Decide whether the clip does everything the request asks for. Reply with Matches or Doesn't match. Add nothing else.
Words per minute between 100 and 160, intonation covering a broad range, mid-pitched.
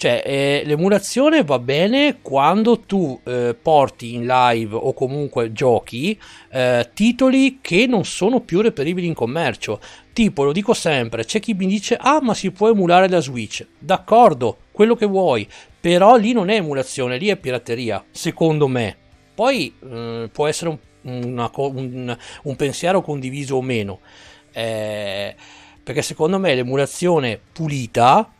Matches